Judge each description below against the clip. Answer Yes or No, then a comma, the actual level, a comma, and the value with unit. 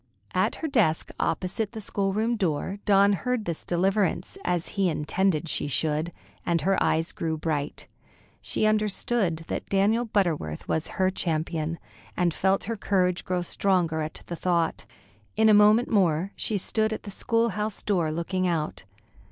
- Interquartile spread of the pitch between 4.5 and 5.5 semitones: No, average, 4.1 semitones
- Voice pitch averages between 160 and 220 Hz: Yes, medium, 185 Hz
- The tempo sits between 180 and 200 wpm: No, average, 160 wpm